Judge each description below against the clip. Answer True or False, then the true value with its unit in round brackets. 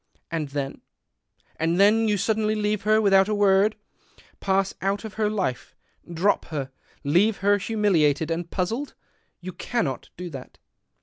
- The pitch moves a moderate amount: True (4.3 semitones)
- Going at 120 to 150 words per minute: True (145 wpm)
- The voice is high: True (195 Hz)